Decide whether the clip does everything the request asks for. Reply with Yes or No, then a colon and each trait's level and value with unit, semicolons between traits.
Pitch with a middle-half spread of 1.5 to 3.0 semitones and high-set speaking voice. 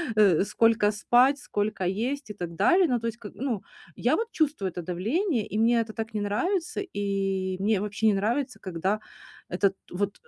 No: average, 4.0 semitones; high, 215 Hz